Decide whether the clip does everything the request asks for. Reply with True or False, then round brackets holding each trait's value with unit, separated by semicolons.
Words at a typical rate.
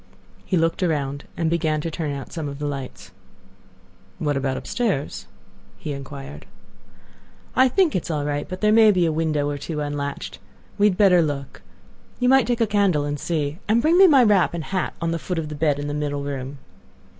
False (210 wpm)